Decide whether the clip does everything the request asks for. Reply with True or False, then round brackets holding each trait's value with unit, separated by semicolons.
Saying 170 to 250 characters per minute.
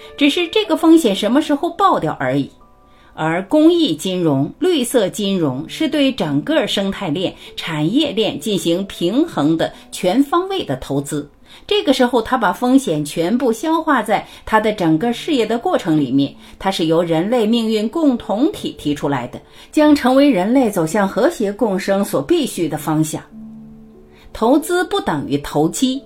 True (245 characters per minute)